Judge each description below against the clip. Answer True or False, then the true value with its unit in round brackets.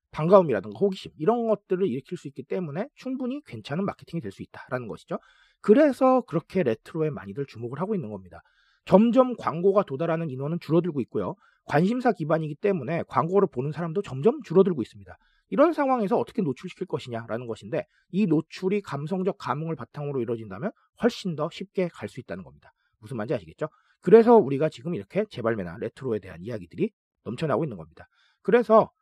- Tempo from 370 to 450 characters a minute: True (445 characters per minute)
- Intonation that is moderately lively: False (6.9 semitones)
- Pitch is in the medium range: True (175 Hz)